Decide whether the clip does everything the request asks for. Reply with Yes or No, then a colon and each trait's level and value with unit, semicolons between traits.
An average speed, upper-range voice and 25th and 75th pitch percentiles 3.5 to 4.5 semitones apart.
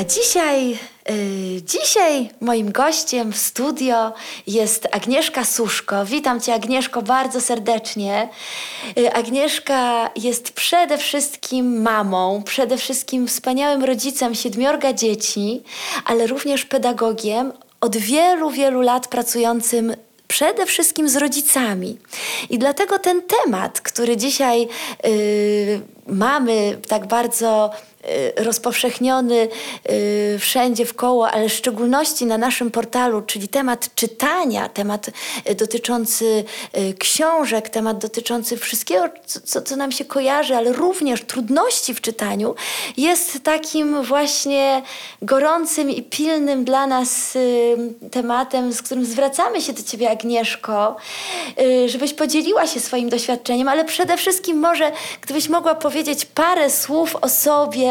Yes: average, 120 wpm; very high, 250 Hz; average, 3.9 semitones